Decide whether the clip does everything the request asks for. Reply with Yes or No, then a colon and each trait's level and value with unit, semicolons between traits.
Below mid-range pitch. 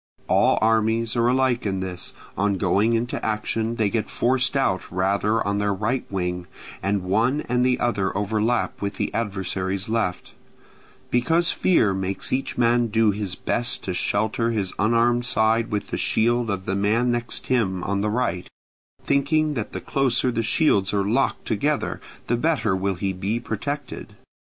Yes: low, 110 Hz